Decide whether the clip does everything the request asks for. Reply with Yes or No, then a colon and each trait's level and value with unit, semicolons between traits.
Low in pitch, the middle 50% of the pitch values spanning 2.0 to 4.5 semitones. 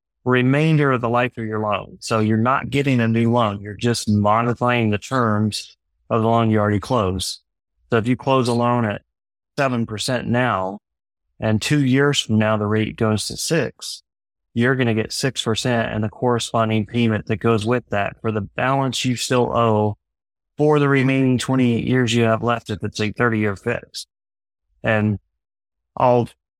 Yes: low, 115 Hz; average, 2.9 semitones